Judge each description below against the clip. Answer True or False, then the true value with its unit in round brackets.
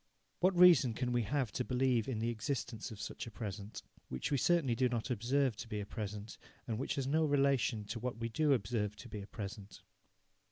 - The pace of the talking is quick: True (215 wpm)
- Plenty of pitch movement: False (4.0 semitones)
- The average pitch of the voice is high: False (120 Hz)